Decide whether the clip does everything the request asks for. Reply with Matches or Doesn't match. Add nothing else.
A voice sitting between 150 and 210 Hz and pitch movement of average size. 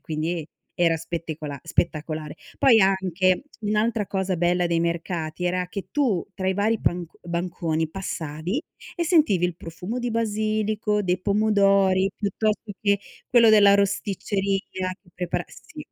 Matches